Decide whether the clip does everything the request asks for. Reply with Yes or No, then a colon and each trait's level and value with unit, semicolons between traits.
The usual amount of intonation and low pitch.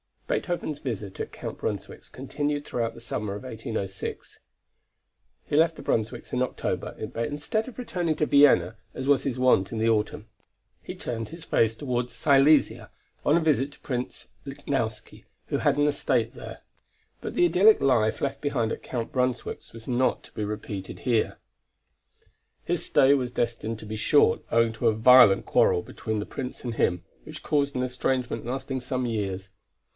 Yes: average, 4.2 semitones; low, 125 Hz